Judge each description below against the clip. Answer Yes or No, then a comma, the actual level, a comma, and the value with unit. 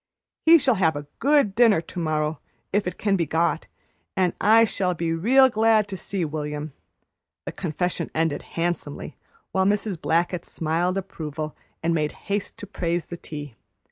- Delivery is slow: No, average, 165 wpm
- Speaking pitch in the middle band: Yes, medium, 175 Hz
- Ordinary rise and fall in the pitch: Yes, average, 4.1 semitones